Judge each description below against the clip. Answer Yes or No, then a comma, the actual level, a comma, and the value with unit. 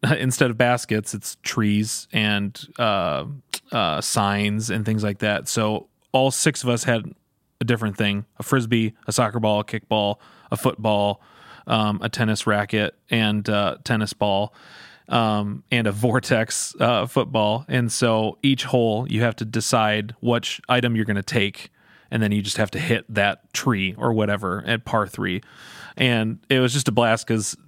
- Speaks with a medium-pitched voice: No, low, 110 Hz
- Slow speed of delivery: No, average, 175 wpm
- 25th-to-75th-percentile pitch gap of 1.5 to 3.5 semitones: Yes, average, 2.7 semitones